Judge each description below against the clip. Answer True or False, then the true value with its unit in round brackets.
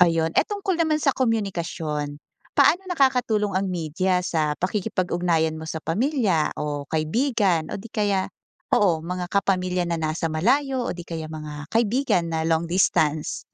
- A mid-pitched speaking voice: True (180 Hz)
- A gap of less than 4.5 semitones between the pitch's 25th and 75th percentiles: False (5.4 semitones)